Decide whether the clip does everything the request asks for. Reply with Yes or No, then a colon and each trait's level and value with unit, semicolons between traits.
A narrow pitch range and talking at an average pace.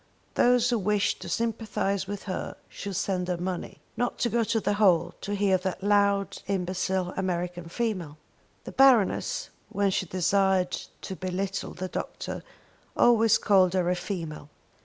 Yes: narrow, 2.2 semitones; average, 155 wpm